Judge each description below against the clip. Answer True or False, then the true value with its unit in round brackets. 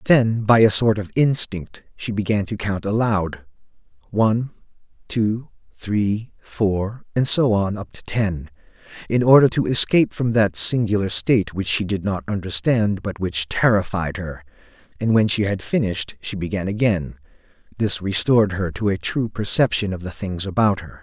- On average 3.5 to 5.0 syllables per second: True (4.7 syllables/s)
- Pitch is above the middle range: False (105 Hz)